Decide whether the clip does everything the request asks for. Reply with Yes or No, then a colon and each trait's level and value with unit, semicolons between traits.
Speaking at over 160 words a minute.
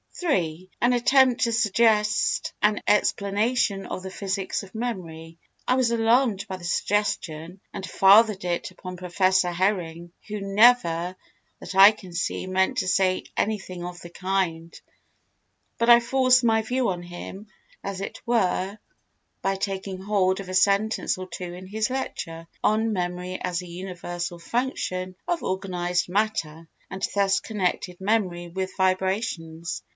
No: average, 145 wpm